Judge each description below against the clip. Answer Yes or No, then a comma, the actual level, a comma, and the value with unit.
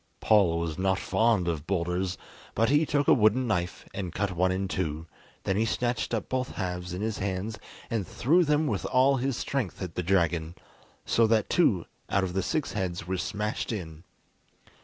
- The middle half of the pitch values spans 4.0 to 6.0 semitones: Yes, average, 4.4 semitones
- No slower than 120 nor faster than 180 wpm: No, average, 190 wpm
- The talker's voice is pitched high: No, very low, 95 Hz